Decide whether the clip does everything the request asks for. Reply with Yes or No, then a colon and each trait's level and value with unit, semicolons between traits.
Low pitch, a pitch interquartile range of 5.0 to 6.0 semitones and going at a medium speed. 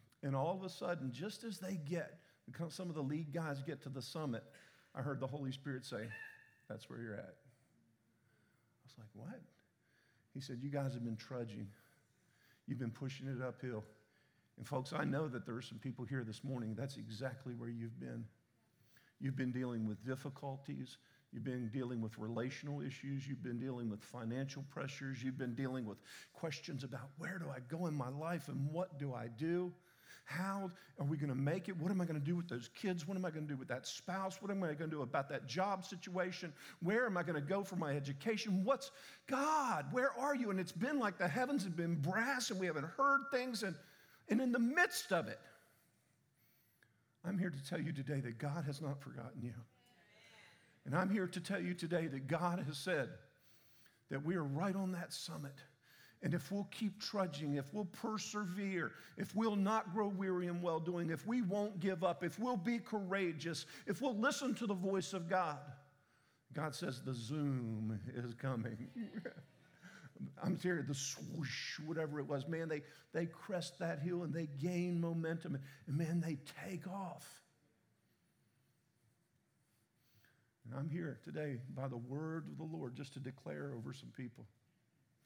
No: medium, 150 Hz; wide, 5.6 semitones; average, 190 wpm